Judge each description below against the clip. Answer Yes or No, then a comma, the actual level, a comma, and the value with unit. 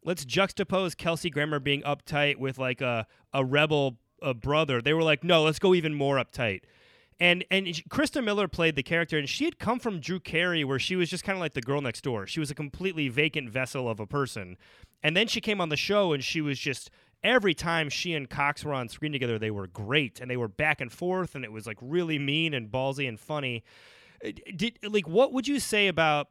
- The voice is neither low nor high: Yes, medium, 150 Hz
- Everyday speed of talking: No, fast, 235 wpm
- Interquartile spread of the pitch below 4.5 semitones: No, average, 4.9 semitones